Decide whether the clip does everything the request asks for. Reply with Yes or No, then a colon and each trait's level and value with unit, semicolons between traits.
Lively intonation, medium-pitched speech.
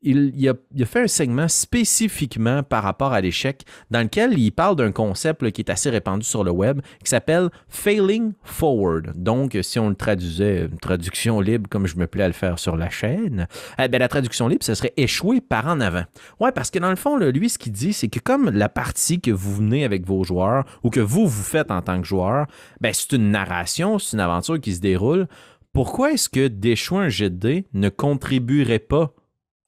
No: wide, 7.5 semitones; low, 120 Hz